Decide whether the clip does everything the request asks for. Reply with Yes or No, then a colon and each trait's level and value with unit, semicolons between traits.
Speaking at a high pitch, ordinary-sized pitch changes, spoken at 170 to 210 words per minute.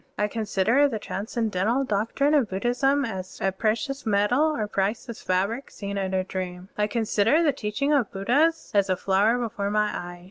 Yes: high, 215 Hz; average, 4.1 semitones; average, 175 wpm